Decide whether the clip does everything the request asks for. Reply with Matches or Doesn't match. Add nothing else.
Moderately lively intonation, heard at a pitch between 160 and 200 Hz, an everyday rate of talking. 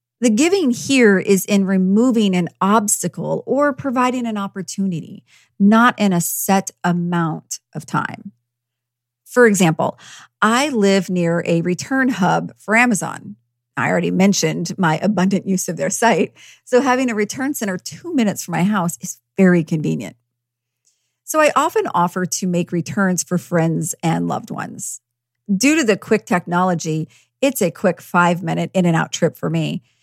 Matches